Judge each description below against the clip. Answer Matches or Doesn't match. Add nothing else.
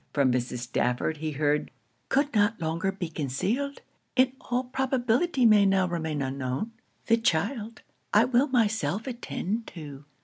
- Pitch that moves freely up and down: Matches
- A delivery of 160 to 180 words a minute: Doesn't match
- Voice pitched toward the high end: Matches